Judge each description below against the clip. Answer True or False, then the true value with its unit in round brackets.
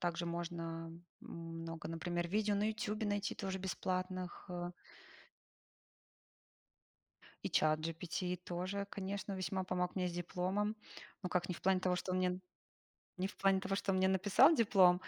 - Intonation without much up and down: True (2.0 semitones)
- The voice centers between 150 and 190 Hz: True (185 Hz)